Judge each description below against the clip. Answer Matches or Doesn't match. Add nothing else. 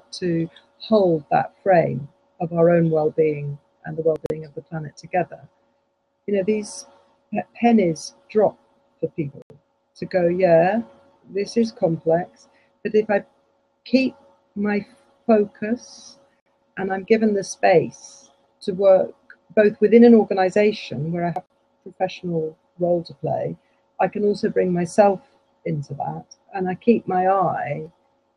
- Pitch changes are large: Doesn't match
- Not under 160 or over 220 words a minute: Doesn't match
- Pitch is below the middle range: Doesn't match